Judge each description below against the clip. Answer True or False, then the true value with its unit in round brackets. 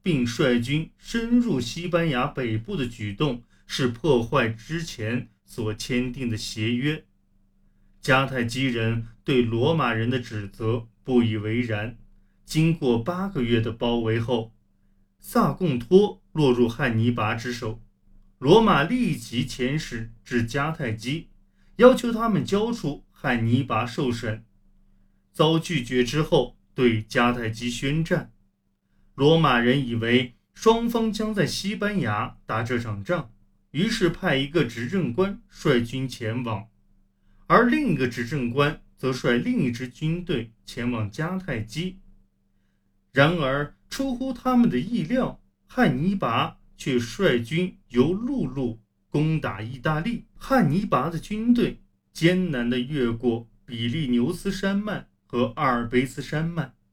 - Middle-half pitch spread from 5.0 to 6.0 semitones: False (6.7 semitones)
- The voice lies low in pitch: True (125 Hz)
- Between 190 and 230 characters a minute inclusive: True (195 characters per minute)